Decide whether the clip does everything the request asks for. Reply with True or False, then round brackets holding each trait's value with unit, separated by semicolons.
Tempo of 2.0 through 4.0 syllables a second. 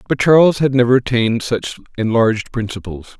False (5.7 syllables/s)